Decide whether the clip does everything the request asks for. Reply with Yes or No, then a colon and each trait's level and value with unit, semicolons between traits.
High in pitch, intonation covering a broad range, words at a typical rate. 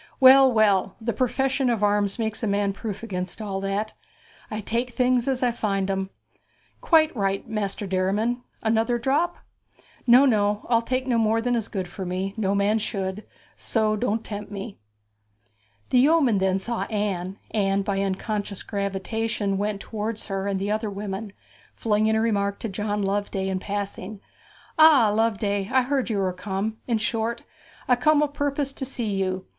No: high, 210 Hz; average, 3.1 semitones; average, 170 wpm